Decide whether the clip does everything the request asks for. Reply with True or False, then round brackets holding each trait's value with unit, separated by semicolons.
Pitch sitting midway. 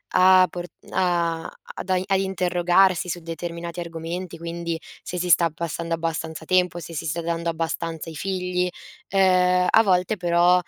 True (175 Hz)